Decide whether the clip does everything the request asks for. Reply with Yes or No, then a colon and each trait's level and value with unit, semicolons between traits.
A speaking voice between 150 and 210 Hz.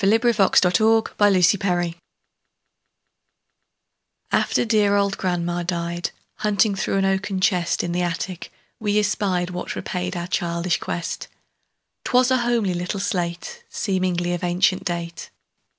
Yes: medium, 185 Hz